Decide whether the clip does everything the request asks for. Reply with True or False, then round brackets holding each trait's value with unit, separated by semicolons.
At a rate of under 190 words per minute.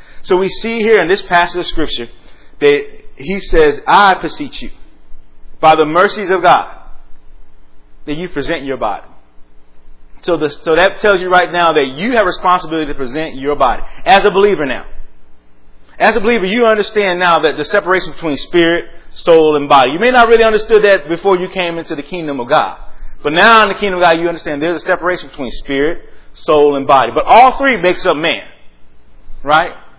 False (195 wpm)